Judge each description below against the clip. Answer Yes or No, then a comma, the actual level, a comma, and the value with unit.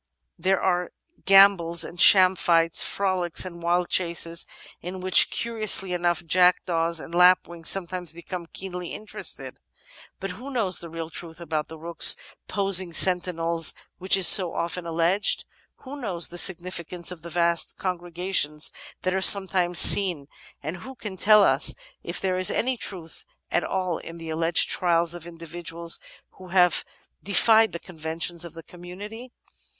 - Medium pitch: Yes, medium, 175 Hz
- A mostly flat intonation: Yes, narrow, 2.0 semitones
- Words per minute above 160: No, average, 155 wpm